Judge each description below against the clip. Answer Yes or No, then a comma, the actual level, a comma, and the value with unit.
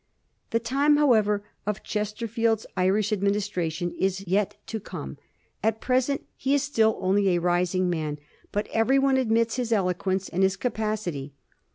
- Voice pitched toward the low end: No, high, 210 Hz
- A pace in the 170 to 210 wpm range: No, average, 155 wpm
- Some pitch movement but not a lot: Yes, average, 3.6 semitones